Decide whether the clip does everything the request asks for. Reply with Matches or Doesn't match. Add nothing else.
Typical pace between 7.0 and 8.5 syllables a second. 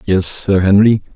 Doesn't match